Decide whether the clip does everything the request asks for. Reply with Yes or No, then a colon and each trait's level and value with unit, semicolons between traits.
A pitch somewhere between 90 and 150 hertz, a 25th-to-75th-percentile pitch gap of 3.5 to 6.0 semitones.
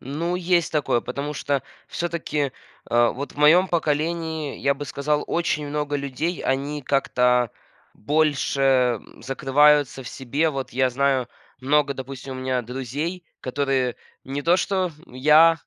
No: medium, 140 Hz; average, 2.7 semitones